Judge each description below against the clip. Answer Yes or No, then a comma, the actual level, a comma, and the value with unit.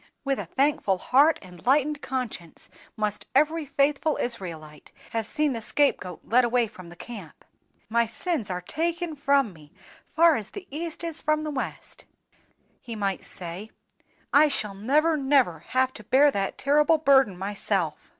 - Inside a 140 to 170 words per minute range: Yes, average, 160 wpm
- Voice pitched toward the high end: Yes, very high, 255 Hz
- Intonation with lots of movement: Yes, wide, 7.0 semitones